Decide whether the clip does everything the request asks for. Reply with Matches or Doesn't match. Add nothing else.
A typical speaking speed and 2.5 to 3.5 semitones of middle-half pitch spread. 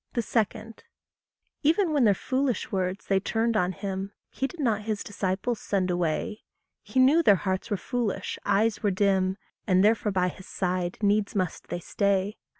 Matches